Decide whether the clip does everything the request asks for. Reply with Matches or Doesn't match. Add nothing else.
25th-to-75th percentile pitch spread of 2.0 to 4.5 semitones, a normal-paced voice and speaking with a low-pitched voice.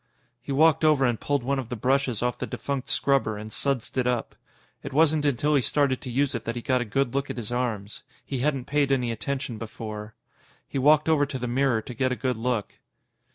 Doesn't match